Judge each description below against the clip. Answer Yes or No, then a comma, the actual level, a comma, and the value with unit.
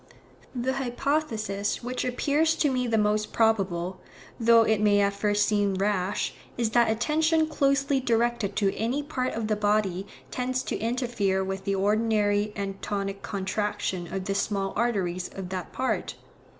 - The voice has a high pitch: Yes, high, 215 Hz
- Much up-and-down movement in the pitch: No, average, 3.8 semitones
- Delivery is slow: No, average, 155 wpm